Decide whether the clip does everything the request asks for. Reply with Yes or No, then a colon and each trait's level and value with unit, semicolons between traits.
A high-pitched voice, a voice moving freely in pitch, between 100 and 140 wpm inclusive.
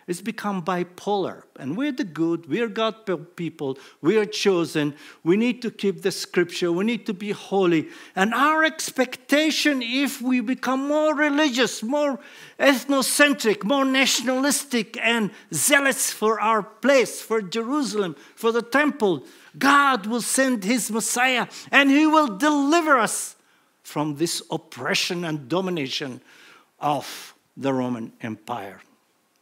Yes: high, 225 Hz; wide, 7.1 semitones; slow, 135 wpm